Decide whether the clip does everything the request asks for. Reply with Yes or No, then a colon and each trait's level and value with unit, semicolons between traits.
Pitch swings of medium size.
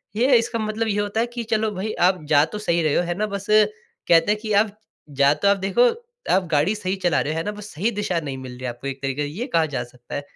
No: wide, 6.2 semitones